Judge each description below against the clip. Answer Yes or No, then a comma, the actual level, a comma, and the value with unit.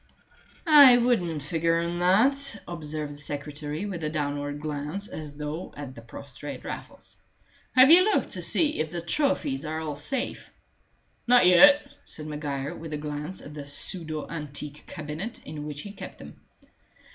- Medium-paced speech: Yes, average, 160 wpm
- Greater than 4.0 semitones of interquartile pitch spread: Yes, average, 5.1 semitones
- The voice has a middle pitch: Yes, medium, 155 Hz